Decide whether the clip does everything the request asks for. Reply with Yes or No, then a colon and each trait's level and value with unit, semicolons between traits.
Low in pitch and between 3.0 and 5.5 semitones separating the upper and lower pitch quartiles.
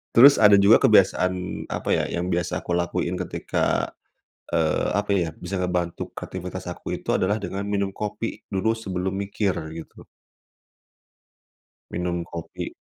No: very low, 95 Hz; narrow, 2.4 semitones